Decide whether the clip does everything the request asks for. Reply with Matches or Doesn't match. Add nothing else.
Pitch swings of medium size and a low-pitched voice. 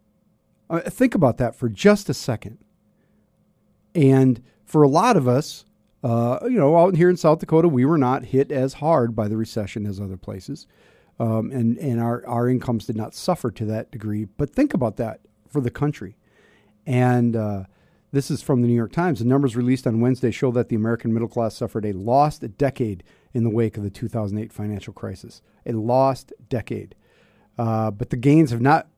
Matches